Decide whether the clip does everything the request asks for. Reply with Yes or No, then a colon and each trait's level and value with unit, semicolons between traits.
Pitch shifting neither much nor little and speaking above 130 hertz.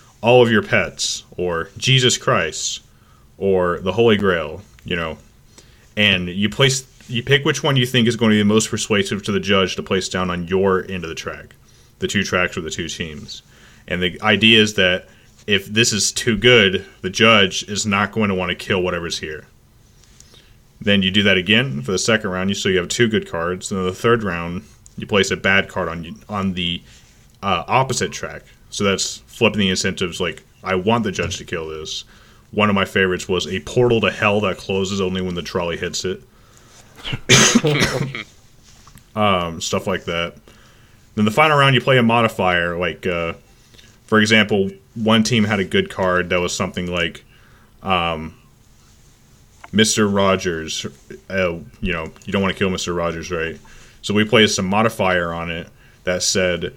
No: average, 3.9 semitones; low, 100 Hz